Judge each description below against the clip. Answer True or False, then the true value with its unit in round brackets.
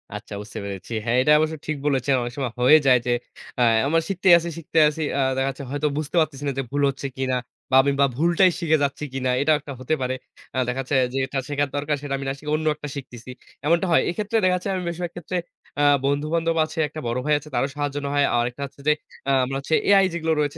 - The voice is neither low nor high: True (145 Hz)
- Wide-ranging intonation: False (3.2 semitones)